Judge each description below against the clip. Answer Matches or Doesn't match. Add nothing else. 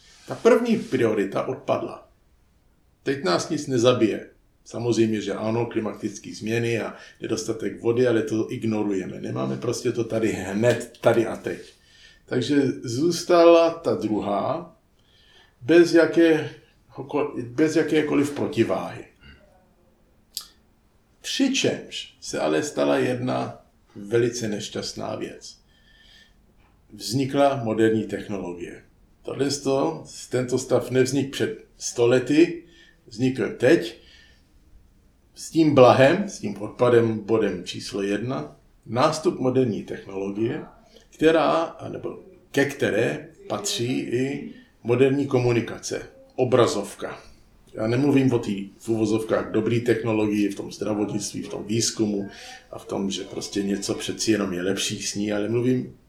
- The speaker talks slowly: Matches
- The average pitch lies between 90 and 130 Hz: Matches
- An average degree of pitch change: Matches